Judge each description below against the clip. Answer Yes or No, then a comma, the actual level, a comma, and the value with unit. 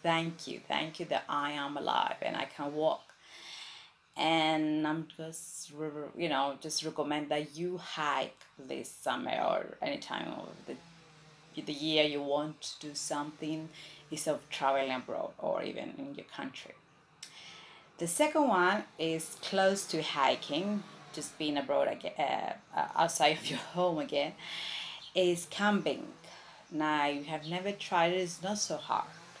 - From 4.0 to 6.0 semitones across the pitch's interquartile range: No, average, 3.1 semitones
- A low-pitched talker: No, medium, 155 Hz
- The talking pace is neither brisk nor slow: Yes, average, 150 wpm